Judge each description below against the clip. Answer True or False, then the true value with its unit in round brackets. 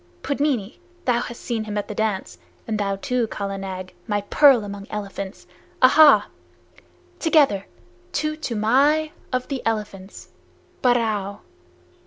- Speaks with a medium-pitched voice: False (220 Hz)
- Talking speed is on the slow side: True (125 wpm)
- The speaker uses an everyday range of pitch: True (4.7 semitones)